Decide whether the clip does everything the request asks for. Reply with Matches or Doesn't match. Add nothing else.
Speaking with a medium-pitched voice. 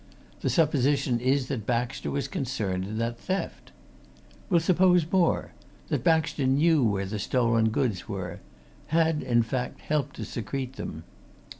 Doesn't match